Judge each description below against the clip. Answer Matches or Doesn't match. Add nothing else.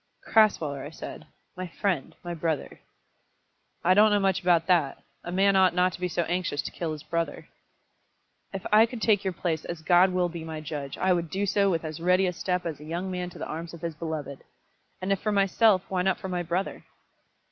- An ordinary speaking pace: Doesn't match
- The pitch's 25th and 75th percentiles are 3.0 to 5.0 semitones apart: Doesn't match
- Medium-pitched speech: Matches